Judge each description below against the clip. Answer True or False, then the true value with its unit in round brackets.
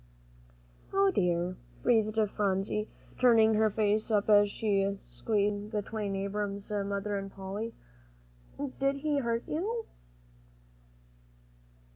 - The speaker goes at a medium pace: False (110 wpm)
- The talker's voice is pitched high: True (210 Hz)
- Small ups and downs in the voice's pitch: True (2.2 semitones)